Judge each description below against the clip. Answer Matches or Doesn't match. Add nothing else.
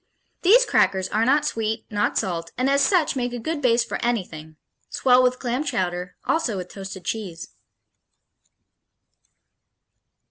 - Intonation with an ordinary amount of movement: Doesn't match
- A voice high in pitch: Matches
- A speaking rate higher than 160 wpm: Doesn't match